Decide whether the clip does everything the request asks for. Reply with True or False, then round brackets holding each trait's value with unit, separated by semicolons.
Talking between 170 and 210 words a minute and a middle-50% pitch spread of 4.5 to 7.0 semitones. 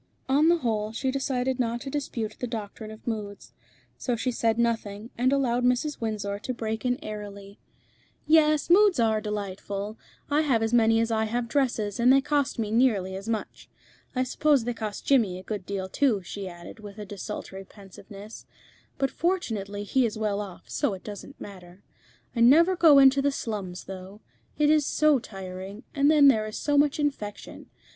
True (185 wpm; 4.8 semitones)